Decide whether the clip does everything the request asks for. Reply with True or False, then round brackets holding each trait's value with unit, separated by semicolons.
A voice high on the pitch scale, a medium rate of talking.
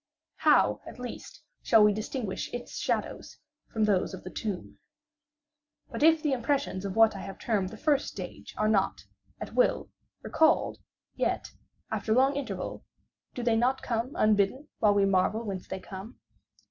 True (220 Hz; 160 wpm)